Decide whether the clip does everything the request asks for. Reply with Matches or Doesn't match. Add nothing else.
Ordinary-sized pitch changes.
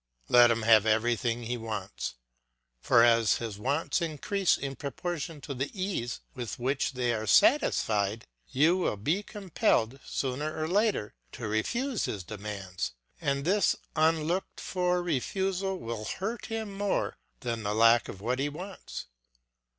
Doesn't match